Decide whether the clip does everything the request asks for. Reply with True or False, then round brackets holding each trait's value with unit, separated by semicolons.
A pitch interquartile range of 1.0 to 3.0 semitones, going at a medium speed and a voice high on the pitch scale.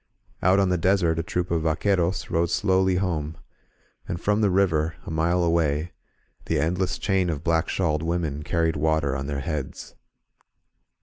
False (2.7 semitones; 165 wpm; 85 Hz)